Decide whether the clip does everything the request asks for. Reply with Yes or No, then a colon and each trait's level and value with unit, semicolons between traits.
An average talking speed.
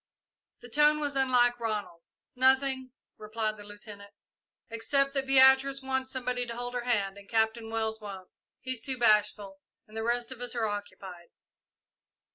Yes: average, 155 wpm